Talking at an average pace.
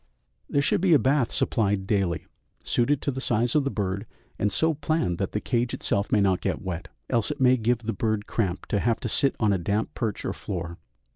No: fast, 225 wpm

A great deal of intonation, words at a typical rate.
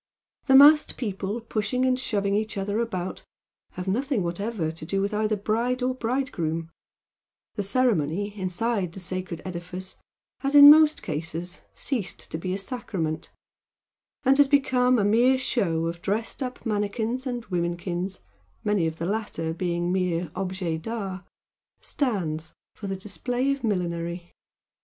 Yes: wide, 5.7 semitones; average, 145 wpm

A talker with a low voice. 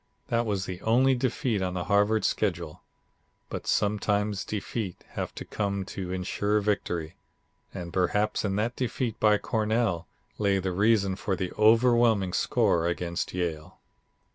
Yes: low, 100 Hz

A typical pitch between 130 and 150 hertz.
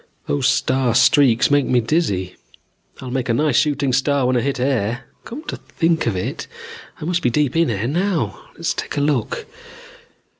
Yes: low, 135 Hz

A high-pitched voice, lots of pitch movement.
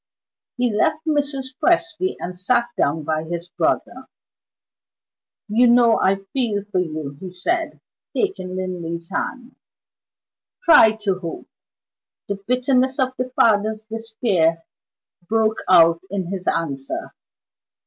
Yes: high, 210 Hz; wide, 6.1 semitones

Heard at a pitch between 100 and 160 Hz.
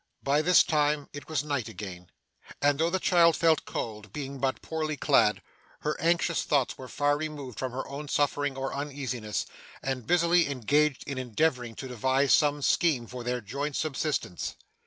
Yes: medium, 140 Hz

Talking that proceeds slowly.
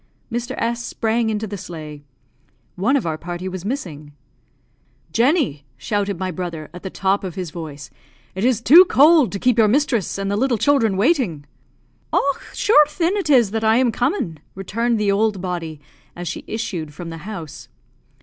No: average, 180 wpm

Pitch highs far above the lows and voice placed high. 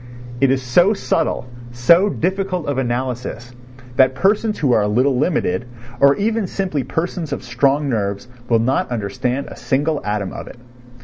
No: wide, 5.7 semitones; low, 135 Hz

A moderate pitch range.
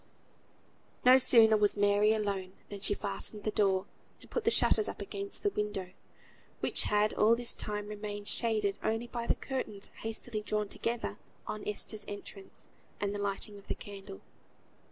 No: narrow, 1.7 semitones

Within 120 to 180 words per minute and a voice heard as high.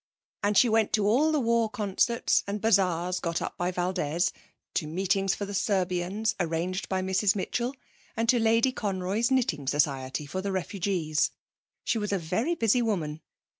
Yes: average, 170 wpm; high, 195 Hz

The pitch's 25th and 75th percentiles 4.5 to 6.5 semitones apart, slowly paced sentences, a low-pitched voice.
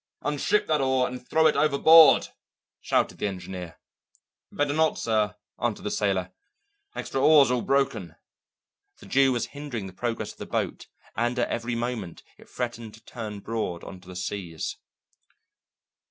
No: average, 5.3 semitones; average, 155 wpm; low, 120 Hz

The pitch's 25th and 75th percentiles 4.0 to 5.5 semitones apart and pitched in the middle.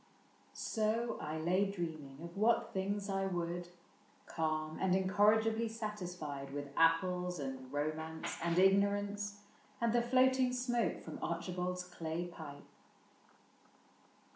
Yes: average, 4.5 semitones; medium, 180 Hz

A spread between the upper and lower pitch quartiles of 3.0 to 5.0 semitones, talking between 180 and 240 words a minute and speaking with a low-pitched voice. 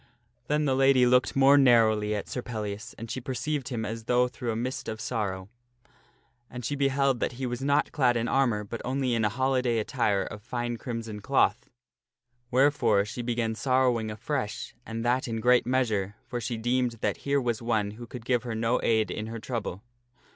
No: narrow, 2.6 semitones; average, 200 wpm; low, 120 Hz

